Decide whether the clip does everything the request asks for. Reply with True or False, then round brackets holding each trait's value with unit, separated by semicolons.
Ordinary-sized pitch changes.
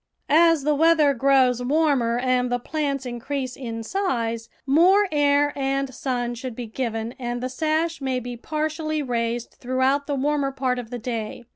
True (3.3 semitones)